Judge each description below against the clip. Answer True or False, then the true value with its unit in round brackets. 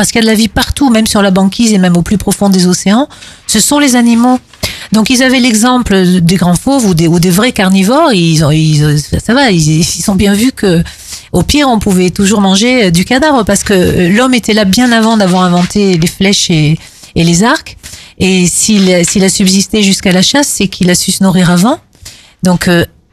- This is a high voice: True (195 Hz)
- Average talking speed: False (225 wpm)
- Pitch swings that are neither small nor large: True (4.3 semitones)